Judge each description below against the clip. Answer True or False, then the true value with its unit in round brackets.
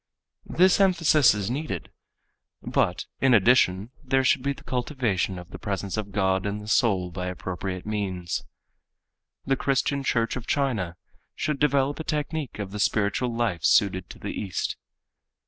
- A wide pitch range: True (6.2 semitones)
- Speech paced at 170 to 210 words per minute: False (155 wpm)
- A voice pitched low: True (110 Hz)